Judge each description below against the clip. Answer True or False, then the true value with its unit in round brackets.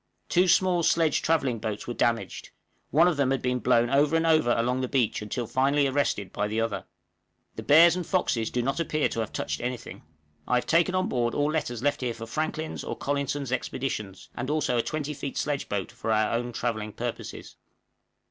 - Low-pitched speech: True (130 Hz)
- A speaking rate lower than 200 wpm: False (205 wpm)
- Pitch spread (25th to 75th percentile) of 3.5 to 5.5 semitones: True (4.6 semitones)